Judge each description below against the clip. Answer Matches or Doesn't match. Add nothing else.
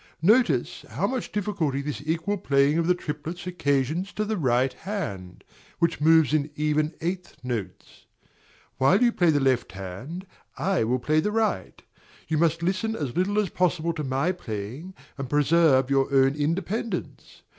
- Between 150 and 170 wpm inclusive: Matches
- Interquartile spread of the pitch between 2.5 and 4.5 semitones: Doesn't match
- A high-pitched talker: Doesn't match